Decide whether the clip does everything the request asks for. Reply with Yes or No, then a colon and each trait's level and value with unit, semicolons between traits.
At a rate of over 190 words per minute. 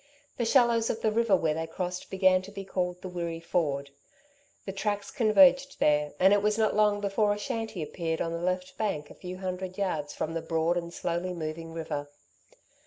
Yes: average, 200 wpm